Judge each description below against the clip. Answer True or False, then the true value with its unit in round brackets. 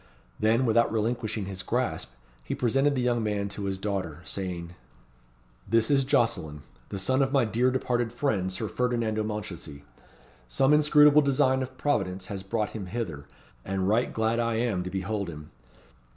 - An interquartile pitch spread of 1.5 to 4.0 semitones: False (4.5 semitones)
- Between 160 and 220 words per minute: True (165 wpm)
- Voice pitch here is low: True (110 Hz)